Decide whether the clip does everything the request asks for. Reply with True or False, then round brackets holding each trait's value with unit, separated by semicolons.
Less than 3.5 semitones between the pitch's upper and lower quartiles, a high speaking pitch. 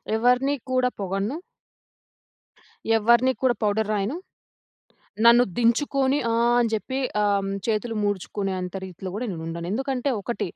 False (3.8 semitones; 230 Hz)